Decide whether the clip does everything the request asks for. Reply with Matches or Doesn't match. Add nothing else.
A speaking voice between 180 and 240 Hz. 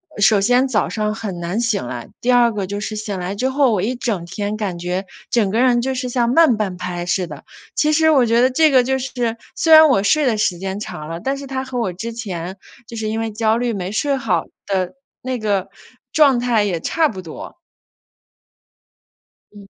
Matches